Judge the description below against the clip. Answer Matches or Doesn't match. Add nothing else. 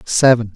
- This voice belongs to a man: Matches